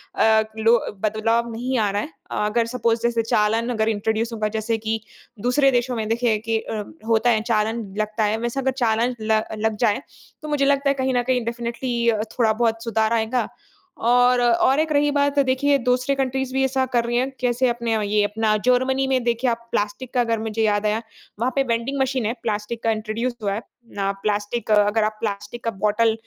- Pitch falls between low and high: No, high, 235 Hz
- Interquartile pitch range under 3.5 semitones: Yes, narrow, 2.5 semitones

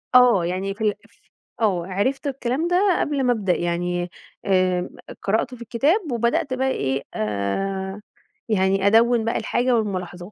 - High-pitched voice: Yes, high, 210 Hz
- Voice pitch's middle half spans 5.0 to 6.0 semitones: Yes, average, 5.3 semitones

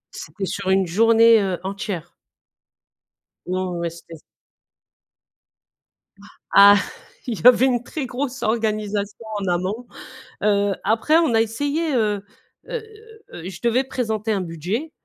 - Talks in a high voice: Yes, high, 215 Hz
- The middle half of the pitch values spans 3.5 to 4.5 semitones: Yes, average, 3.8 semitones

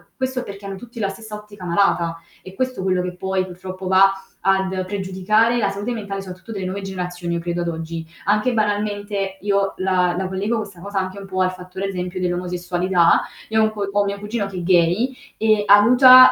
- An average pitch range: No, narrow, 2.2 semitones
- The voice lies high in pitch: Yes, high, 195 Hz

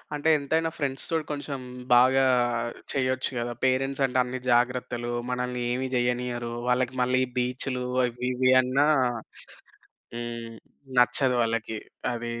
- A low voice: Yes, low, 125 Hz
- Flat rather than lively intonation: Yes, narrow, 1.5 semitones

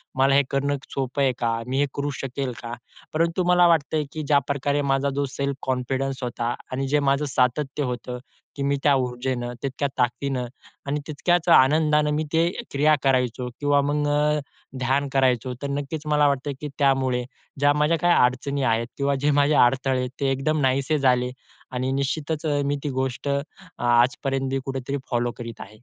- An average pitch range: No, narrow, 2.1 semitones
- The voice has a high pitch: No, medium, 140 Hz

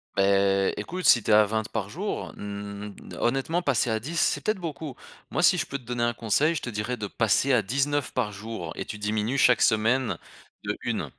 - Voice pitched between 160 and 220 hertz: No, low, 115 Hz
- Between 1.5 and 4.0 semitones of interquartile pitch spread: No, average, 4.9 semitones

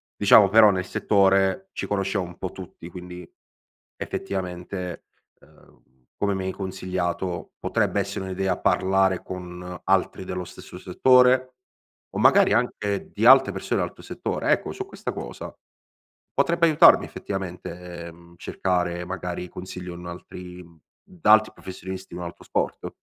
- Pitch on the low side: Yes, very low, 95 Hz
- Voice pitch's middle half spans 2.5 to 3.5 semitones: No, narrow, 1.9 semitones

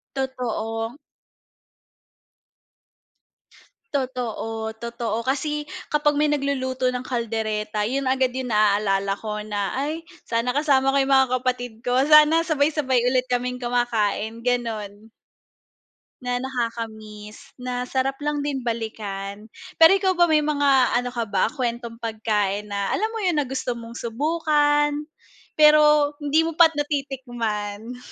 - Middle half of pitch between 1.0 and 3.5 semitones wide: No, average, 4.3 semitones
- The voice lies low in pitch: No, very high, 250 Hz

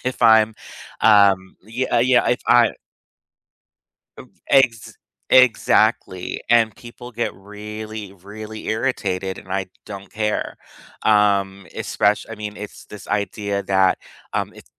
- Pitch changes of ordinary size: No, narrow, 2.3 semitones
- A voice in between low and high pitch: No, low, 105 Hz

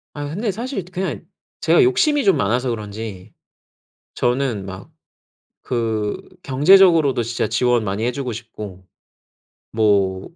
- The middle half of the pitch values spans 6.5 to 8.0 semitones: Yes, wide, 7.2 semitones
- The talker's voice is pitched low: Yes, low, 120 Hz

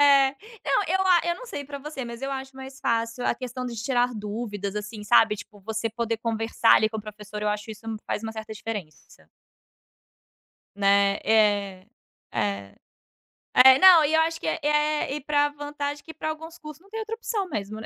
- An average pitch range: No, wide, 5.7 semitones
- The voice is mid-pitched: No, high, 235 Hz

